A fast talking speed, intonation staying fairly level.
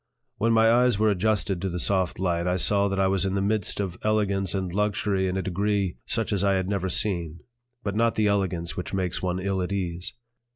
Yes: fast, 225 wpm; narrow, 2.1 semitones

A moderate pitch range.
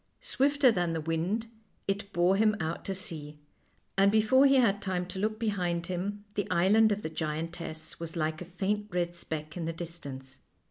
Yes: average, 3.9 semitones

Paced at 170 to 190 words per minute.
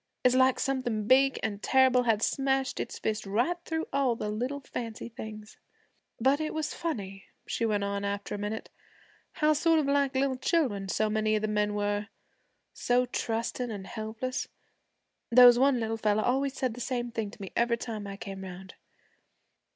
Yes: average, 180 wpm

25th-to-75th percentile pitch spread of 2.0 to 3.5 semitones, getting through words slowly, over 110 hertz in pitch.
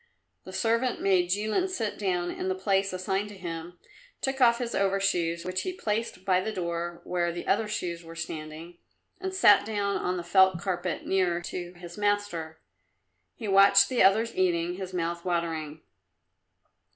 No: average, 3.0 semitones; average, 165 wpm; medium, 185 Hz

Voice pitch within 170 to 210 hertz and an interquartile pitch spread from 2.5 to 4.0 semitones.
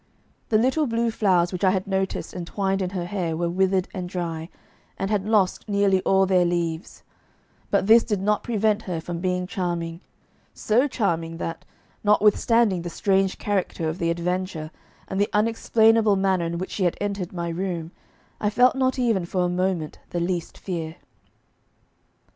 Yes: high, 190 Hz; average, 3.2 semitones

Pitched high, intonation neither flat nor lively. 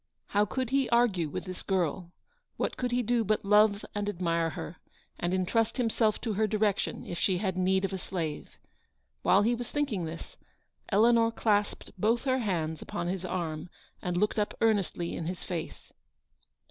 Yes: high, 200 Hz; average, 4.1 semitones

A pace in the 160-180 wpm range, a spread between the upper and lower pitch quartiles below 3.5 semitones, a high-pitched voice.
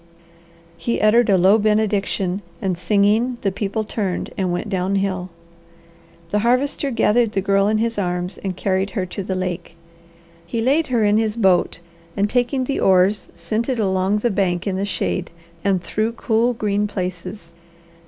Yes: average, 165 wpm; average, 3.0 semitones; high, 200 Hz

